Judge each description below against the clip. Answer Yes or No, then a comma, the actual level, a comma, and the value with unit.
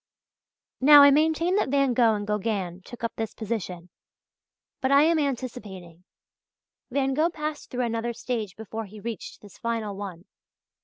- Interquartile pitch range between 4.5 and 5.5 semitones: Yes, average, 5.2 semitones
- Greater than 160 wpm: No, average, 155 wpm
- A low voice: No, high, 230 Hz